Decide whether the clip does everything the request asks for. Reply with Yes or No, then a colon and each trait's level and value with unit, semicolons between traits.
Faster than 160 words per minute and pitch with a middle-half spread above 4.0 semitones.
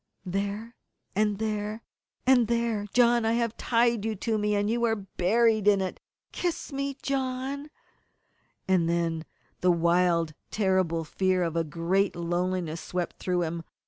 No: average, 155 wpm; average, 4.9 semitones